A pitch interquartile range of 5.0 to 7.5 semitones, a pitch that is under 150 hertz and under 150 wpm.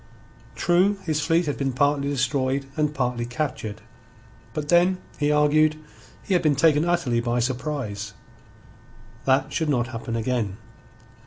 No: average, 3.9 semitones; medium, 140 Hz; average, 140 wpm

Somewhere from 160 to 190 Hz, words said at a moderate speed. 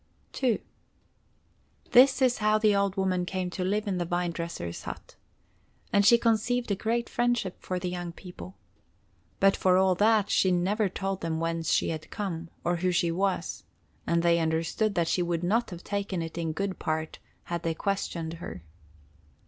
Yes: medium, 185 Hz; average, 180 wpm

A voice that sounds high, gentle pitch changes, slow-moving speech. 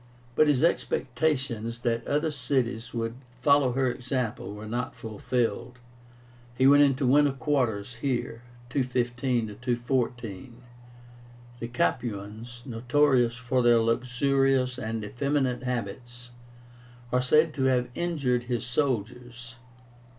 No: low, 125 Hz; narrow, 2.3 semitones; slow, 110 wpm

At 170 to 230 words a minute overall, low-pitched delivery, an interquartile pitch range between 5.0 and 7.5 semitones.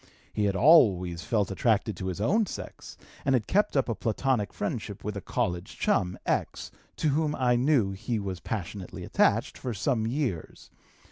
Yes: average, 175 wpm; low, 110 Hz; wide, 5.4 semitones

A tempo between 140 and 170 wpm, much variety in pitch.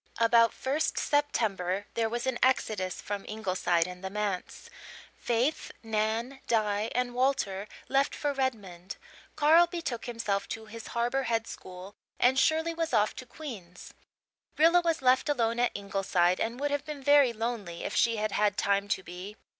No: average, 160 wpm; average, 4.8 semitones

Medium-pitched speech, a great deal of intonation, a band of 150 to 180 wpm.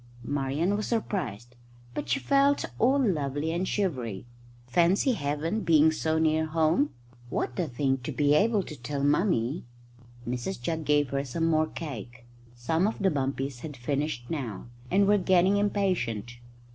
Yes: medium, 155 Hz; wide, 5.7 semitones; average, 155 wpm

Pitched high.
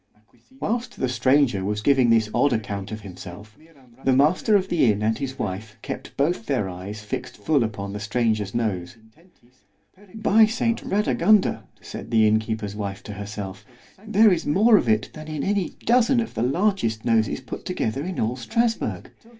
No: low, 120 Hz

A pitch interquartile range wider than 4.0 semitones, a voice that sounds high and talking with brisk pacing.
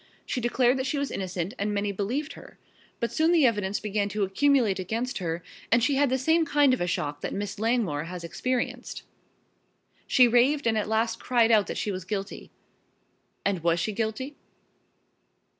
No: average, 4.7 semitones; high, 220 Hz; average, 190 wpm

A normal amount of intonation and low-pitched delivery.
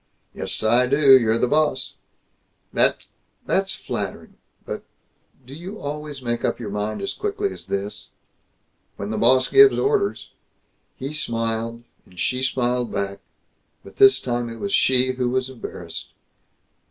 Yes: average, 4.6 semitones; low, 125 Hz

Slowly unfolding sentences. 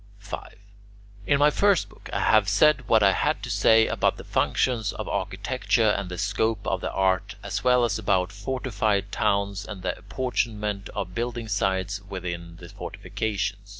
No: average, 170 wpm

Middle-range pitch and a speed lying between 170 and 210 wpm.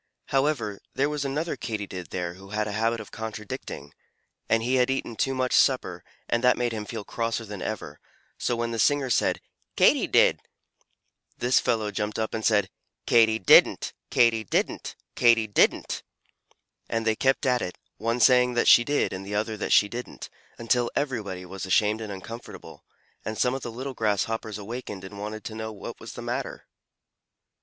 No: low, 115 Hz; average, 180 wpm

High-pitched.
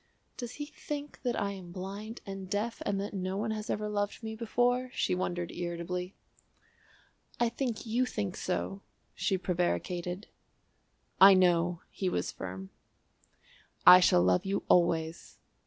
Yes: high, 195 Hz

